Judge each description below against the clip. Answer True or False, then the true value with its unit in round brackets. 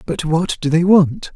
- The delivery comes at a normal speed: False (220 wpm)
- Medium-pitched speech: True (165 Hz)